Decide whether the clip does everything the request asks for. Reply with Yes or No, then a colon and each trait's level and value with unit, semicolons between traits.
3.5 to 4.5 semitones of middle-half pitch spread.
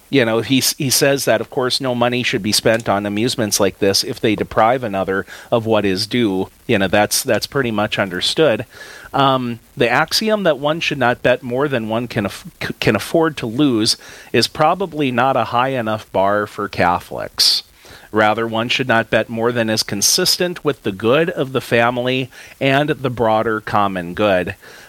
Yes: average, 4.0 semitones